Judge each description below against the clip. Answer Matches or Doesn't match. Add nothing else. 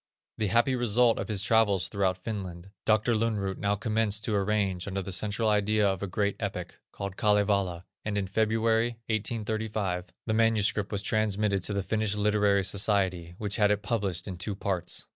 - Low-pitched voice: Matches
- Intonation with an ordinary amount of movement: Doesn't match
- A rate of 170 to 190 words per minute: Matches